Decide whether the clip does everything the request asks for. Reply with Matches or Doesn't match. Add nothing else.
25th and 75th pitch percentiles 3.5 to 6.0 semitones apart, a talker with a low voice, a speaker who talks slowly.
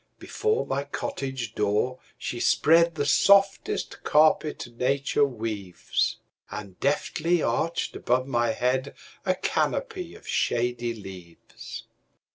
Matches